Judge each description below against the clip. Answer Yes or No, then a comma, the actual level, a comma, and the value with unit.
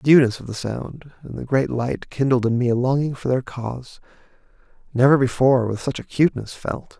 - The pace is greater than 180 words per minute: Yes, average, 195 wpm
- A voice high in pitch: No, low, 130 Hz